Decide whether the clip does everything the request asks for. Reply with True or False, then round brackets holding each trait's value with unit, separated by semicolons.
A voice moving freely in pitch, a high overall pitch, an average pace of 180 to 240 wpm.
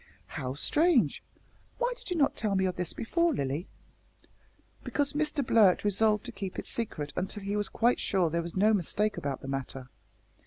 True (6.1 semitones; 205 Hz; 190 wpm)